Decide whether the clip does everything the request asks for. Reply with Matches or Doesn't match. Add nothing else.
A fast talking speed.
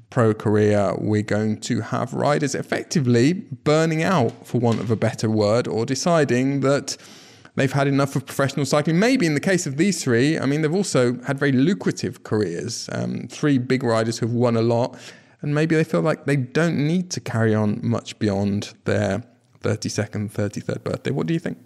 Doesn't match